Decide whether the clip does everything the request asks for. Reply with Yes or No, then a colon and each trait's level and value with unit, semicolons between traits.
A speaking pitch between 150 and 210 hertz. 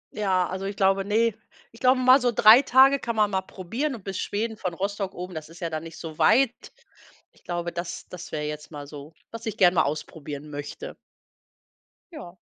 Yes: high, 190 Hz